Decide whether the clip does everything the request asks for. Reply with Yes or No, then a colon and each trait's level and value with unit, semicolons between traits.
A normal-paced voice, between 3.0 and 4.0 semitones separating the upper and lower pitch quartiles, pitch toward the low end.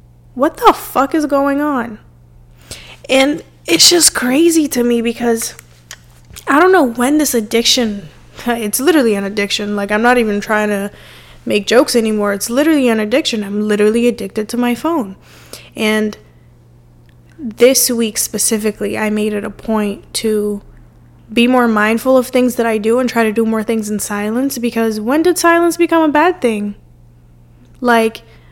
No: average, 160 wpm; average, 3.6 semitones; high, 225 Hz